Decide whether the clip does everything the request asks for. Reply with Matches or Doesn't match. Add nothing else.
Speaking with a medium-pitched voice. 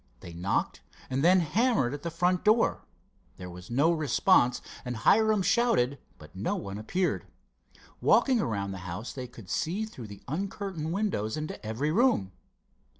Matches